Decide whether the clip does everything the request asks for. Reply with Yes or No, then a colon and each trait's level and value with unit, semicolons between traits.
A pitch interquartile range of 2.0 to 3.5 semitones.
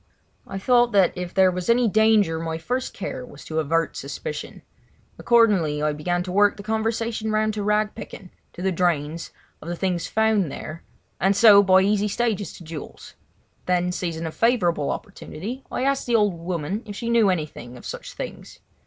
No: average, 4.6 semitones